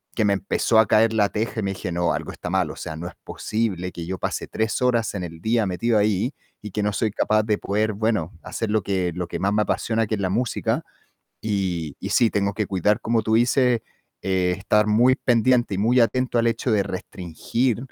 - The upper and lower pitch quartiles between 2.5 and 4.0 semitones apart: Yes, average, 3.1 semitones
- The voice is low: Yes, low, 105 Hz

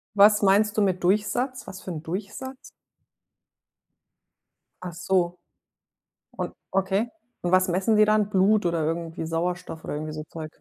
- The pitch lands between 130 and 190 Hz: Yes, medium, 185 Hz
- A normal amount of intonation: Yes, average, 3.6 semitones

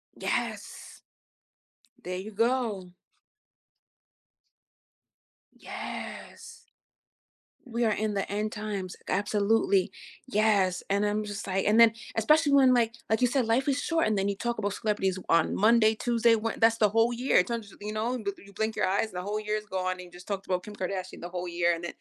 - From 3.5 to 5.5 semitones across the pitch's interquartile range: No, average, 3.0 semitones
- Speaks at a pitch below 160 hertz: No, high, 210 Hz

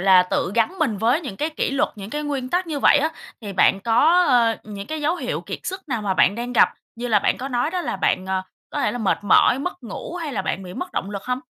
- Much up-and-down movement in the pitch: Yes, wide, 6.9 semitones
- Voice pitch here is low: No, high, 240 Hz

